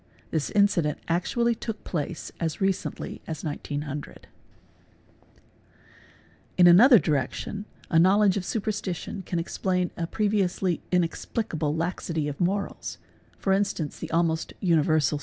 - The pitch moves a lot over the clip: No, average, 3.9 semitones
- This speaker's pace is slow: Yes, slow, 120 wpm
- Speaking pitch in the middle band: Yes, medium, 175 Hz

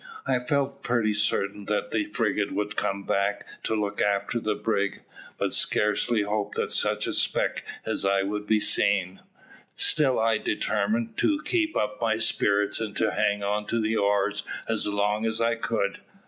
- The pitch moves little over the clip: Yes, narrow, 1.7 semitones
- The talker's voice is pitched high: No, low, 105 Hz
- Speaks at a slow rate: No, average, 175 wpm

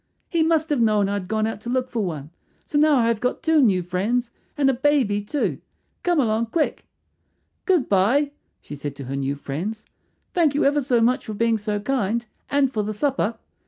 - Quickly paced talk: Yes, fast, 210 wpm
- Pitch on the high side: Yes, high, 230 Hz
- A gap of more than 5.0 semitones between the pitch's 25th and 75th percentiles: Yes, wide, 5.5 semitones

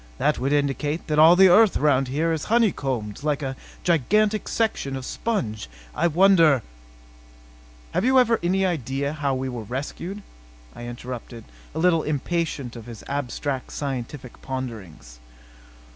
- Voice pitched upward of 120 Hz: Yes, medium, 140 Hz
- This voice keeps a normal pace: Yes, average, 145 wpm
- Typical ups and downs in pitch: No, wide, 5.8 semitones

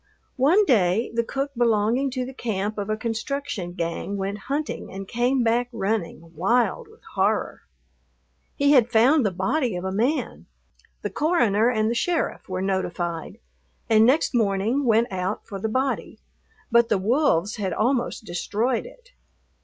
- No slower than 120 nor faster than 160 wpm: Yes, average, 155 wpm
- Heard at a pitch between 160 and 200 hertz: No, high, 230 Hz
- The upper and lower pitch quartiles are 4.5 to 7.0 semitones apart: Yes, average, 5.0 semitones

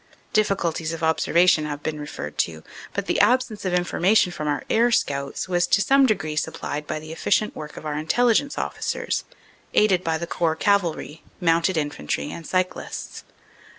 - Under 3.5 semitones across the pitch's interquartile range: No, average, 4.7 semitones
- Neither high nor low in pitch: Yes, medium, 165 Hz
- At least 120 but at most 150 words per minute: No, average, 165 wpm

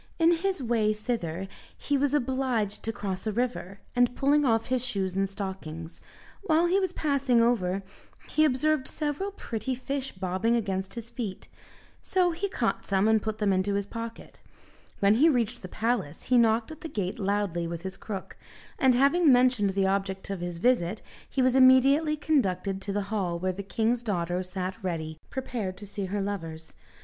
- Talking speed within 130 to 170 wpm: No, average, 180 wpm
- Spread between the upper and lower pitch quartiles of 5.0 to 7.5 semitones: Yes, average, 5.3 semitones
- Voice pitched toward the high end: Yes, high, 220 Hz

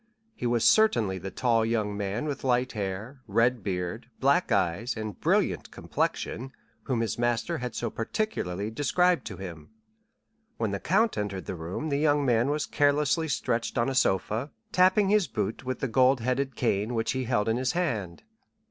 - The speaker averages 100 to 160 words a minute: No, average, 175 wpm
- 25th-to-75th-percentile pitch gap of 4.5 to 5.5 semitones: Yes, average, 5.1 semitones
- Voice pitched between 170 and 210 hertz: No, low, 120 Hz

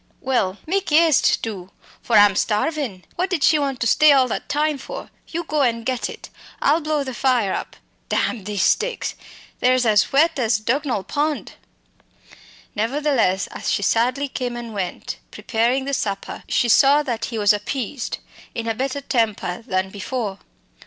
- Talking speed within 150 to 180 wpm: Yes, average, 165 wpm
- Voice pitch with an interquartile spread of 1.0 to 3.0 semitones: No, average, 5.0 semitones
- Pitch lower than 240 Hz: No, very high, 250 Hz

